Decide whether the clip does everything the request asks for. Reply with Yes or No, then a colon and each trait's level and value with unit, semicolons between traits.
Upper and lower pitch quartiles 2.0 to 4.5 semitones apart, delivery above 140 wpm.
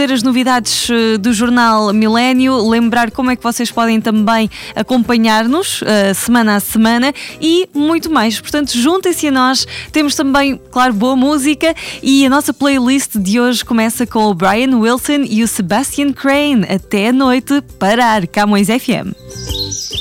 Yes: average, 3.9 semitones; average, 150 wpm